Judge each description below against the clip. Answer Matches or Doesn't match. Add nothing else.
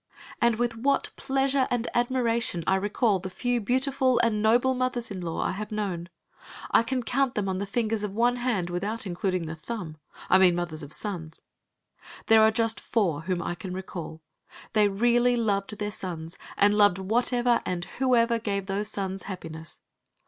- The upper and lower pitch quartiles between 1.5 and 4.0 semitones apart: Doesn't match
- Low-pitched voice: Doesn't match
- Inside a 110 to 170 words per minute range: Doesn't match